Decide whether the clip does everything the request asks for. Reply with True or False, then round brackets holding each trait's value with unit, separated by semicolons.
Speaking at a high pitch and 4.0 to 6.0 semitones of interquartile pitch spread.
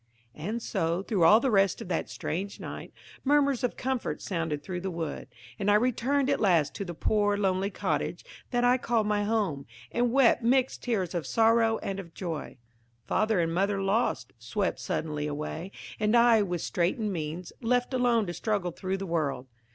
True (200 Hz; 5.2 semitones)